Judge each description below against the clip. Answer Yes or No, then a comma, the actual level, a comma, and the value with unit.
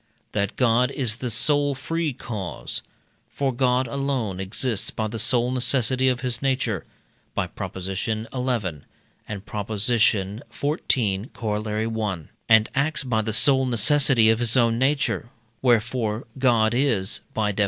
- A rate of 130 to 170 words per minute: Yes, average, 140 wpm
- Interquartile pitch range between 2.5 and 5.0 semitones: Yes, average, 3.3 semitones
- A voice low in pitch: Yes, low, 120 Hz